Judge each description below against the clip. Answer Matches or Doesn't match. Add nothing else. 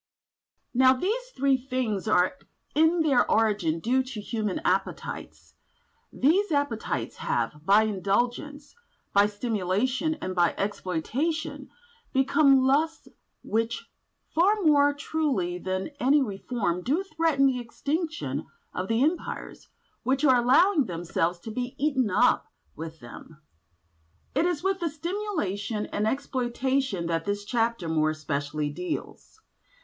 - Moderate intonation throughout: Doesn't match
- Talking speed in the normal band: Doesn't match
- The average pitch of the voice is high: Matches